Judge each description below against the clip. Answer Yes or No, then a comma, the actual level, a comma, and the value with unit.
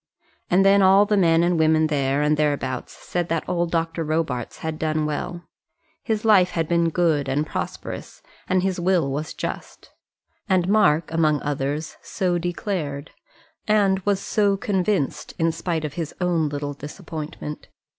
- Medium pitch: Yes, medium, 165 Hz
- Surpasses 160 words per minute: No, average, 155 wpm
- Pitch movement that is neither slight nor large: Yes, average, 3.4 semitones